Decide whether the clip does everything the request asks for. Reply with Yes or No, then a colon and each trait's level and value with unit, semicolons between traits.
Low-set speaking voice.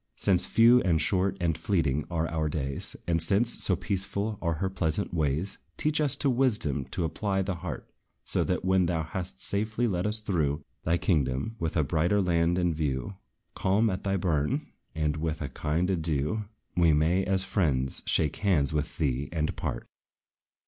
Yes: very low, 85 Hz